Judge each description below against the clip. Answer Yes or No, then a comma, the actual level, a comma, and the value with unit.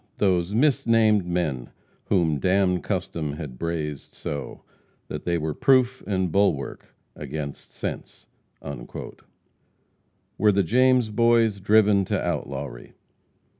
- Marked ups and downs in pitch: Yes, wide, 6.1 semitones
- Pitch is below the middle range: Yes, very low, 90 Hz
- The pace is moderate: No, slow, 105 wpm